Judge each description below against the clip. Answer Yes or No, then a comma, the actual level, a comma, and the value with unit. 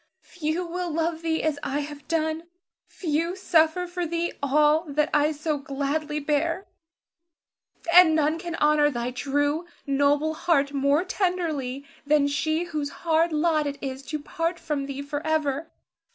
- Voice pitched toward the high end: Yes, very high, 305 Hz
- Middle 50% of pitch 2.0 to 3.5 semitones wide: Yes, narrow, 2.5 semitones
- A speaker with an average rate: Yes, average, 150 wpm